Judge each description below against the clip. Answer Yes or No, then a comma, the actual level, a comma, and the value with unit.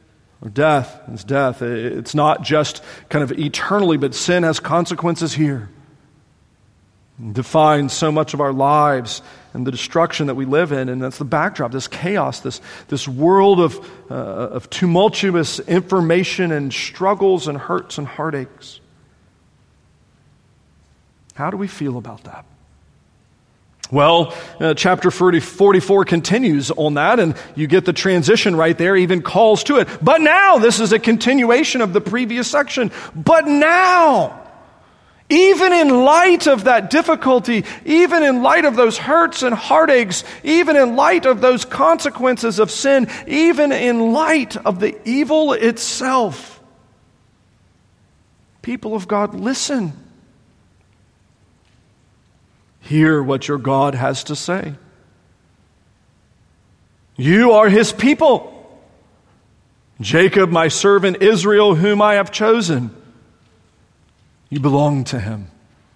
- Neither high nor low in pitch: Yes, medium, 165 Hz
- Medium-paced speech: No, slow, 130 wpm